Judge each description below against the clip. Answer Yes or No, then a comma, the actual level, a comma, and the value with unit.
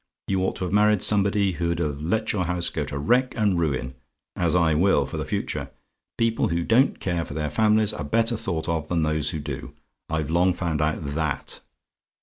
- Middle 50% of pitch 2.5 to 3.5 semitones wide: No, average, 4.5 semitones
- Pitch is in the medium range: No, very low, 85 Hz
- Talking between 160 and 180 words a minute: No, fast, 205 wpm